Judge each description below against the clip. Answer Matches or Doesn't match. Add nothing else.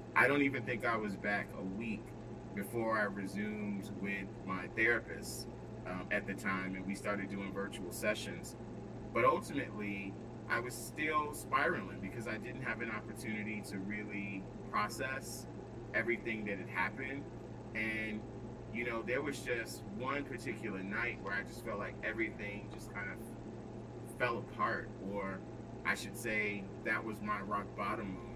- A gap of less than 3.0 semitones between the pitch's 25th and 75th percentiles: Matches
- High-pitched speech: Doesn't match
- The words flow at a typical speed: Matches